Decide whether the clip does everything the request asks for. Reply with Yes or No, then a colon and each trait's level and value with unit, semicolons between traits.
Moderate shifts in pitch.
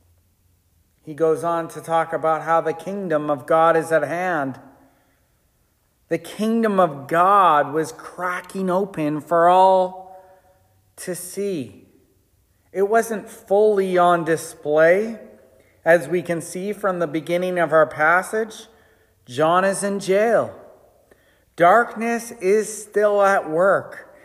Yes: average, 4.0 semitones